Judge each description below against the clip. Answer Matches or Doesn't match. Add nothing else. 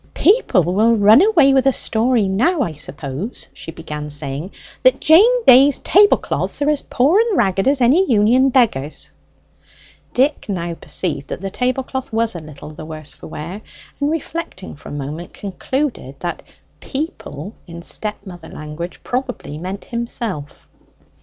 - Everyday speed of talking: Matches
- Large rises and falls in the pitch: Matches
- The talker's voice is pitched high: Matches